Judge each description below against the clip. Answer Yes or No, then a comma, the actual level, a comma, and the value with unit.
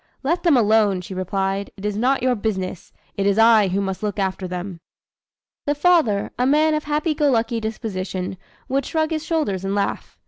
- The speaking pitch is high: Yes, high, 215 Hz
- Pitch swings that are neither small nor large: No, wide, 6.4 semitones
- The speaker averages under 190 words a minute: No, average, 195 wpm